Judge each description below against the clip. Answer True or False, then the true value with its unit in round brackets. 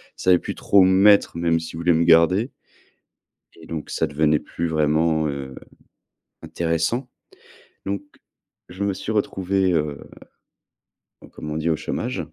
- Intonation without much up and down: False (3.2 semitones)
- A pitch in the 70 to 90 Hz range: True (85 Hz)